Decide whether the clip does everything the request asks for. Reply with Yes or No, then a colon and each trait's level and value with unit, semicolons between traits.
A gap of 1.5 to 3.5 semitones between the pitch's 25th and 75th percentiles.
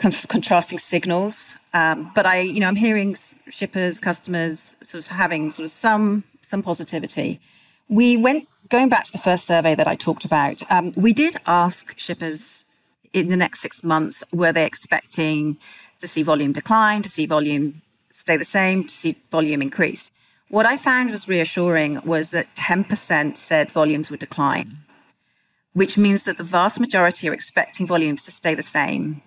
No: average, 4.5 semitones